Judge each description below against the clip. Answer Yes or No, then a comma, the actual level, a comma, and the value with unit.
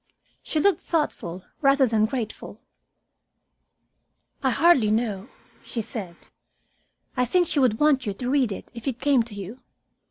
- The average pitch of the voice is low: No, high, 245 Hz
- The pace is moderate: Yes, average, 150 wpm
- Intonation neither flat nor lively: Yes, average, 4.5 semitones